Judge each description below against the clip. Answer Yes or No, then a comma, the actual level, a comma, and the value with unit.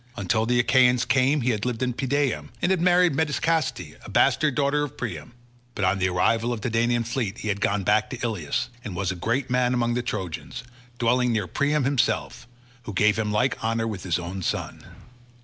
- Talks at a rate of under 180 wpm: No, fast, 205 wpm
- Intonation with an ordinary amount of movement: Yes, average, 3.9 semitones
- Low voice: Yes, low, 120 Hz